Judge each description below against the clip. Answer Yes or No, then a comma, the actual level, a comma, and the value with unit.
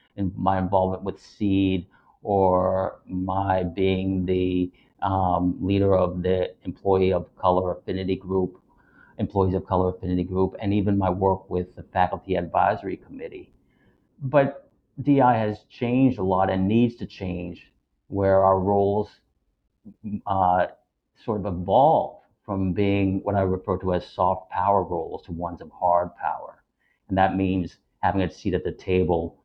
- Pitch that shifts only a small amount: Yes, narrow, 1.3 semitones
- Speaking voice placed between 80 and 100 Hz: Yes, very low, 95 Hz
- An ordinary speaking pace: Yes, average, 150 wpm